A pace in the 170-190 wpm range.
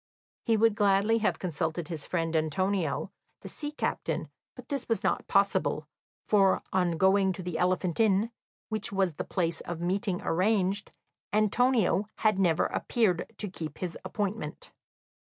No: average, 155 wpm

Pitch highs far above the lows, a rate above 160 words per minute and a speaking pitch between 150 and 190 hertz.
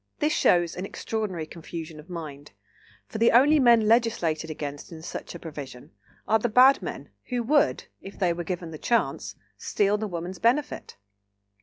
Yes: wide, 6.2 semitones; average, 170 wpm; medium, 185 Hz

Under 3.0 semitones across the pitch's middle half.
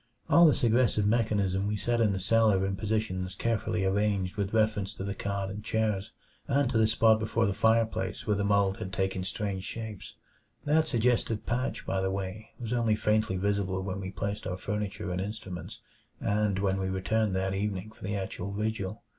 Yes: narrow, 2.4 semitones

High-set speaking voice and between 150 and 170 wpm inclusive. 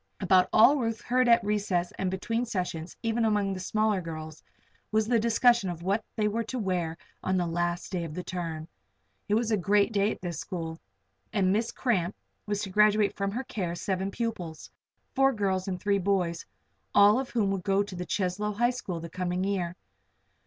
No: high, 195 Hz; average, 195 wpm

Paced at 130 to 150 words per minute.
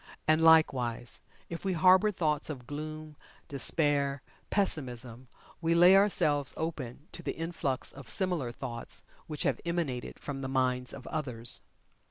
Yes: average, 140 wpm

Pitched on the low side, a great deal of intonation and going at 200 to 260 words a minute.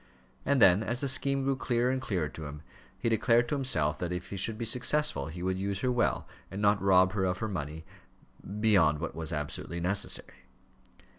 Yes: low, 100 Hz; wide, 5.9 semitones; fast, 205 wpm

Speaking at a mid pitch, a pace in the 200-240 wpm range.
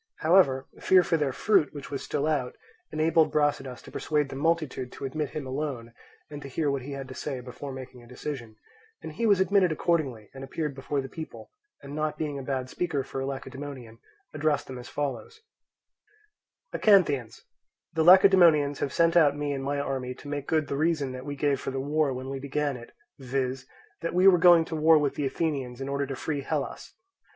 Yes: medium, 145 Hz; fast, 205 wpm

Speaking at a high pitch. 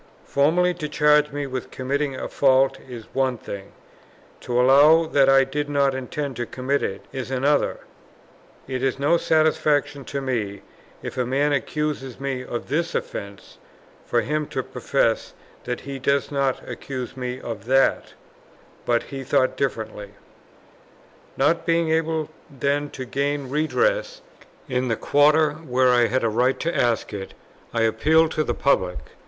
No: low, 135 Hz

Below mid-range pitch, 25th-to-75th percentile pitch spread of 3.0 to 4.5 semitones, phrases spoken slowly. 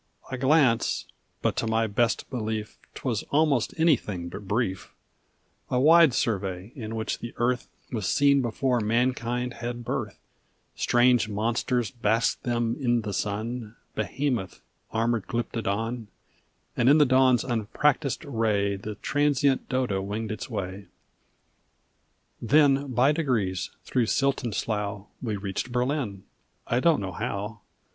Yes: low, 120 Hz; average, 3.6 semitones; slow, 130 wpm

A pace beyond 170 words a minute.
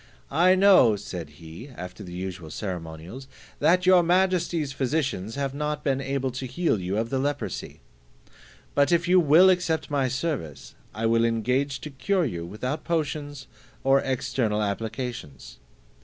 No: average, 150 wpm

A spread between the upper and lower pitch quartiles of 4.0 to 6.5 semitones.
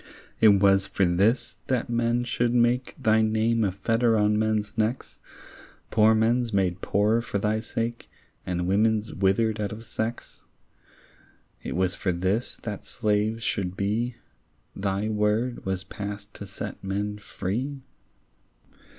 No: narrow, 2.6 semitones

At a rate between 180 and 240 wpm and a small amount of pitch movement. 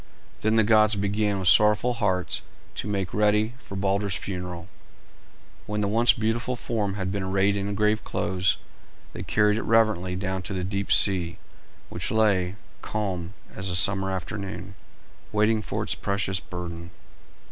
No: average, 155 wpm; narrow, 2.3 semitones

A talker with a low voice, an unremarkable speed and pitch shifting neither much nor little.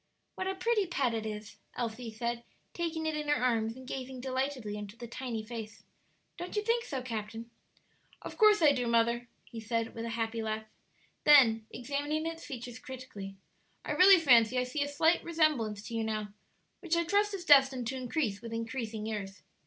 No: high, 245 Hz; average, 190 wpm; average, 5.0 semitones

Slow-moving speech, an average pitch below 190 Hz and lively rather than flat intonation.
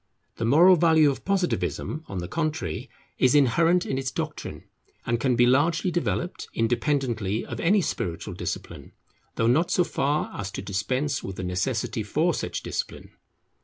No: average, 160 wpm; low, 135 Hz; wide, 6.4 semitones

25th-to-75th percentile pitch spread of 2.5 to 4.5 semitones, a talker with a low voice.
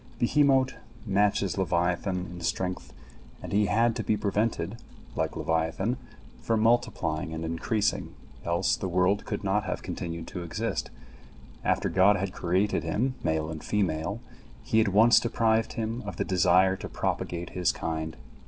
Yes: average, 4.2 semitones; very low, 95 Hz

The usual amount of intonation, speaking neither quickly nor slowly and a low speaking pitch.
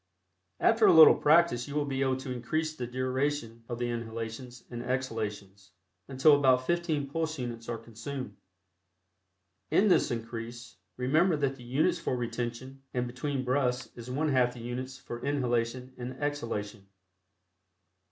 Yes: average, 3.1 semitones; average, 150 wpm; low, 125 Hz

